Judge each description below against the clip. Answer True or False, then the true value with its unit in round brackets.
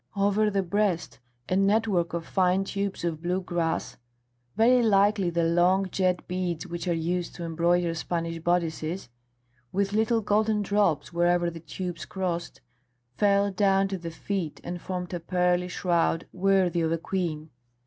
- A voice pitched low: False (180 Hz)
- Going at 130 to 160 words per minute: True (155 wpm)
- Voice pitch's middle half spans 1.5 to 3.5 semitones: True (2.5 semitones)